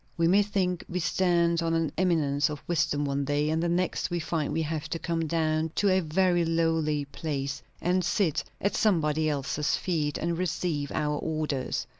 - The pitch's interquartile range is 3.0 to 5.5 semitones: No, narrow, 2.6 semitones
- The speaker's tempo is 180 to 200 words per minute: Yes, average, 185 wpm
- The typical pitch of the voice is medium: Yes, medium, 165 Hz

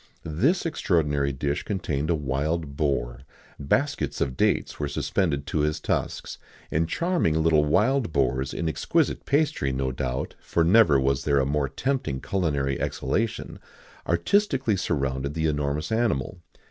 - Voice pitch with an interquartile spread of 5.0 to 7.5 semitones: Yes, wide, 5.6 semitones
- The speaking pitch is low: Yes, very low, 75 Hz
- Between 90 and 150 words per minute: Yes, average, 140 wpm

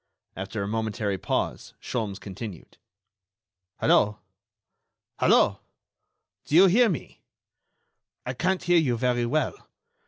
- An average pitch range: No, wide, 7.9 semitones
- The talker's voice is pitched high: No, low, 120 Hz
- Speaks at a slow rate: Yes, slow, 105 wpm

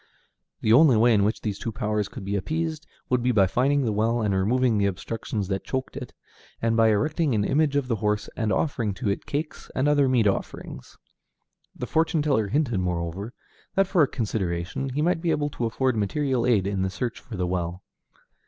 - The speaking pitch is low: Yes, low, 115 Hz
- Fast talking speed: Yes, fast, 210 wpm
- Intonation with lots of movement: Yes, wide, 5.7 semitones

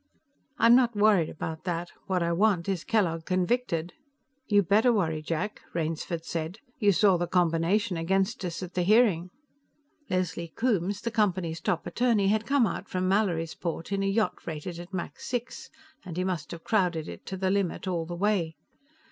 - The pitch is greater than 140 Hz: Yes, medium, 185 Hz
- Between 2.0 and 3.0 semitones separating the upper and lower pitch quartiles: No, average, 3.6 semitones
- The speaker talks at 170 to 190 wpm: Yes, average, 175 wpm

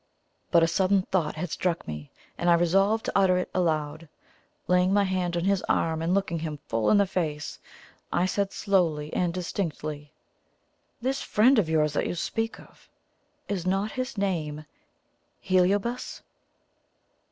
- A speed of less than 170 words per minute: Yes, average, 155 wpm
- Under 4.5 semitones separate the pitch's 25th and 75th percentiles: Yes, average, 3.7 semitones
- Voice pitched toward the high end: No, medium, 180 Hz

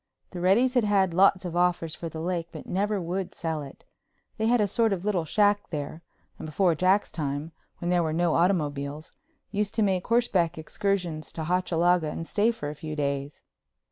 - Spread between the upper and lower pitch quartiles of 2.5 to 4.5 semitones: Yes, average, 3.9 semitones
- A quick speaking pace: No, average, 195 wpm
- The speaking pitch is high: No, medium, 175 Hz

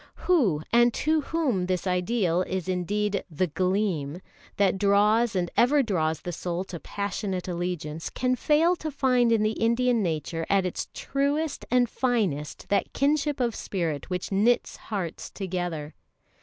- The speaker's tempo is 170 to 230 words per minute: No, average, 145 wpm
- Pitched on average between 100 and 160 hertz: No, high, 200 Hz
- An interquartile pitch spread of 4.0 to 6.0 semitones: Yes, wide, 5.5 semitones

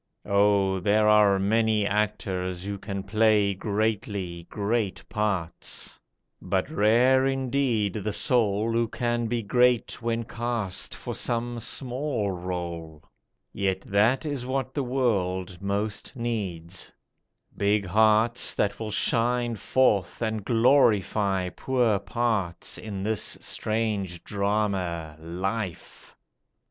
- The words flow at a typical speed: No, slow, 110 wpm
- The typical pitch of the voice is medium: No, low, 105 Hz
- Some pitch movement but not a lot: Yes, average, 3.3 semitones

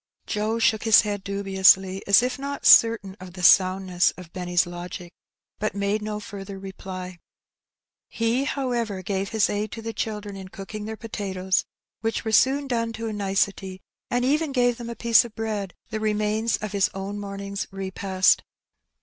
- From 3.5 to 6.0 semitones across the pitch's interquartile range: No, average, 2.8 semitones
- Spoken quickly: No, average, 175 wpm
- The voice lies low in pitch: No, high, 205 Hz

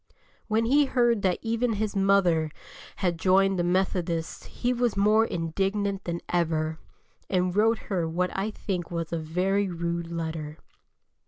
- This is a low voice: No, medium, 185 Hz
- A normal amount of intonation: Yes, average, 3.6 semitones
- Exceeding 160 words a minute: No, average, 150 wpm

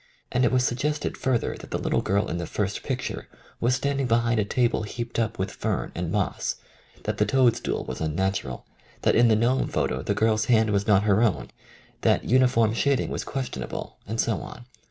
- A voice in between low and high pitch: No, low, 115 Hz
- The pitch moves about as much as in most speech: Yes, average, 3.6 semitones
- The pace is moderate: No, fast, 210 wpm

